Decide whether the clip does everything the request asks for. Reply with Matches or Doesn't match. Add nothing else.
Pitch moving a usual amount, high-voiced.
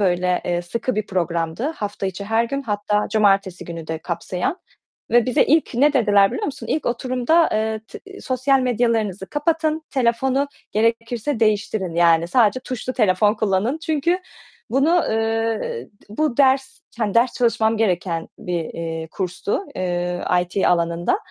Doesn't match